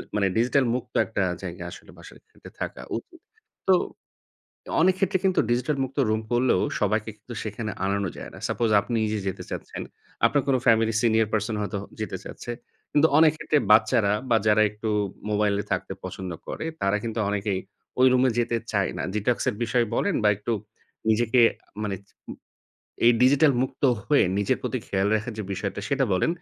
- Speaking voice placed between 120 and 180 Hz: No, low, 110 Hz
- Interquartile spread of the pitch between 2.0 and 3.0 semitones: No, average, 3.7 semitones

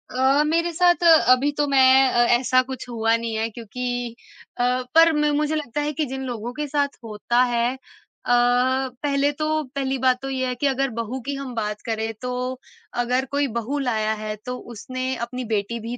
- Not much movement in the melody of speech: No, average, 3.2 semitones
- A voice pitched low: No, very high, 255 Hz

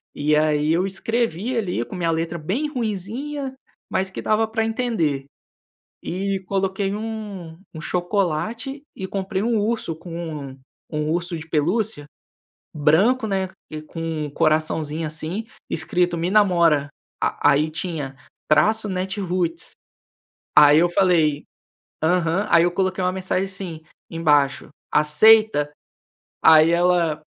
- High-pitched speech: No, medium, 180 Hz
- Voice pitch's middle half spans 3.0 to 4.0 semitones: No, average, 4.4 semitones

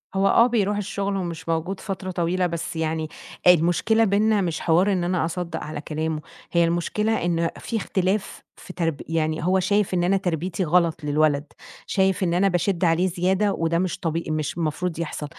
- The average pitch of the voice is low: No, medium, 175 Hz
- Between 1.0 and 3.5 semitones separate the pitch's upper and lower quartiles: Yes, average, 2.8 semitones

